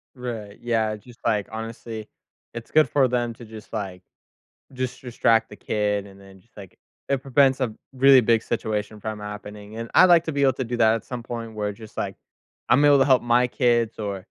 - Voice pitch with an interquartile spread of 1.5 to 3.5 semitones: Yes, average, 2.9 semitones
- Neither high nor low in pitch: No, low, 115 Hz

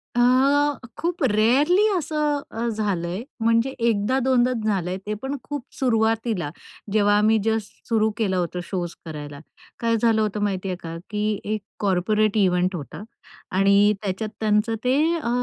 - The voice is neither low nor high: No, high, 215 Hz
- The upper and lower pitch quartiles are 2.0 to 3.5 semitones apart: Yes, average, 3.2 semitones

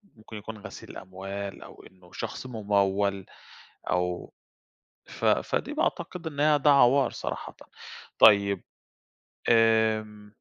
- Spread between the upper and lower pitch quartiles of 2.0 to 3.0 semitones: Yes, narrow, 2.5 semitones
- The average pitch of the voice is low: Yes, low, 105 Hz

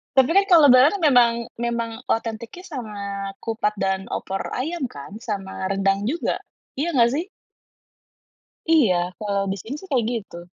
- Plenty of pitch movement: Yes, wide, 5.7 semitones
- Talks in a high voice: Yes, high, 230 Hz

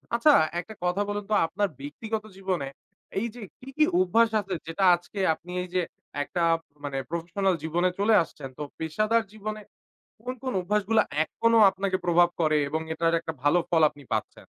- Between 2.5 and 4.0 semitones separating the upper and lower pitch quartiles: No, average, 4.5 semitones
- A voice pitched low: No, medium, 185 Hz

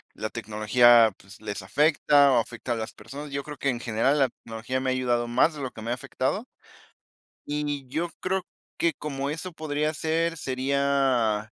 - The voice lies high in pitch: No, low, 130 Hz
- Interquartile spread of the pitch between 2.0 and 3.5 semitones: No, average, 4.0 semitones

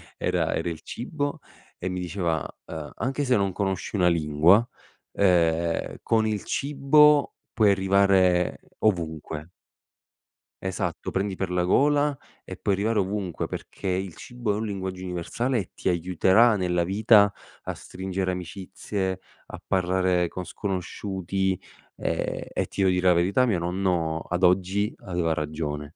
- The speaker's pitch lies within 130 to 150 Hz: No, very low, 95 Hz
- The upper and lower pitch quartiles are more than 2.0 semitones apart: Yes, average, 2.7 semitones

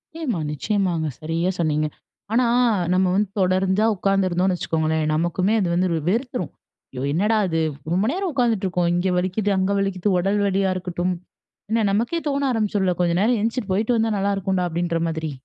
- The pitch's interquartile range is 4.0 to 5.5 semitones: No, average, 3.5 semitones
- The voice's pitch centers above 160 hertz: Yes, high, 190 Hz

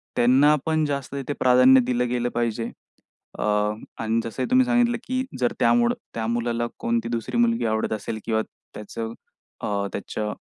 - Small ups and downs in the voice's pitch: No, average, 3.5 semitones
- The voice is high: No, low, 120 Hz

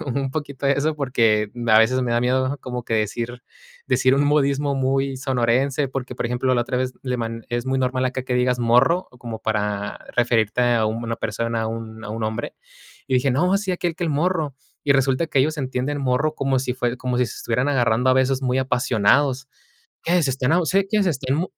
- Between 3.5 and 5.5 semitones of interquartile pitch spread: No, average, 2.7 semitones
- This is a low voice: Yes, low, 130 Hz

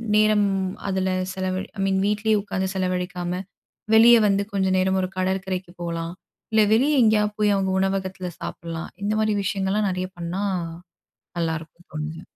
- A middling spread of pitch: No, narrow, 2.3 semitones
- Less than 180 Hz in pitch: No, high, 190 Hz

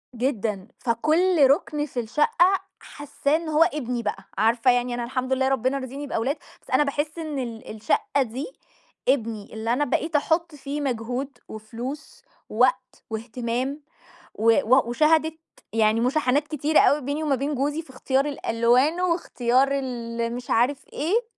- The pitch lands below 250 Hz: No, very high, 265 Hz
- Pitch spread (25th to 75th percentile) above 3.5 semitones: Yes, average, 4.0 semitones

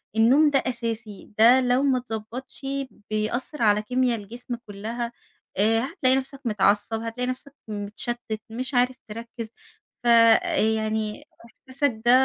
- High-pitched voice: Yes, high, 235 Hz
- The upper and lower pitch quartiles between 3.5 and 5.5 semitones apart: No, average, 2.7 semitones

